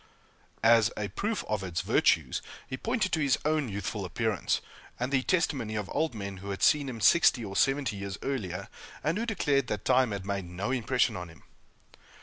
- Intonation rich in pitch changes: Yes, wide, 5.9 semitones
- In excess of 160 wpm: Yes, average, 190 wpm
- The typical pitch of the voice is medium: No, low, 115 Hz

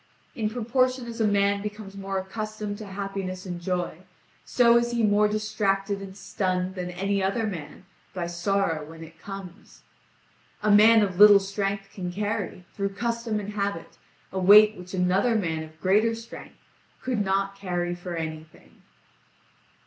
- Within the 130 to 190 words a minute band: Yes, average, 155 wpm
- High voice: Yes, high, 195 Hz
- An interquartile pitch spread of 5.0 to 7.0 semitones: No, narrow, 2.5 semitones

